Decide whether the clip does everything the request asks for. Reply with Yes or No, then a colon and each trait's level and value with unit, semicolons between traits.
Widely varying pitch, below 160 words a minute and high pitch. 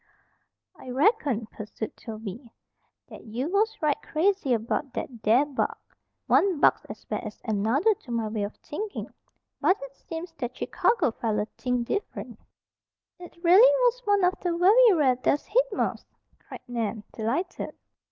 Yes: wide, 8.7 semitones; average, 150 wpm; very high, 280 Hz